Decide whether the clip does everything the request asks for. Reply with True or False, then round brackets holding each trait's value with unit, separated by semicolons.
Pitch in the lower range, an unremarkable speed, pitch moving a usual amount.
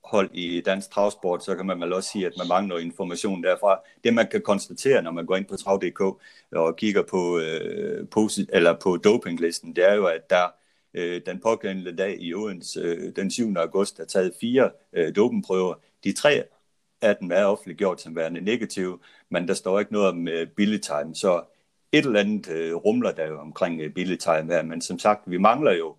True (90 Hz; 200 wpm; 3.1 semitones)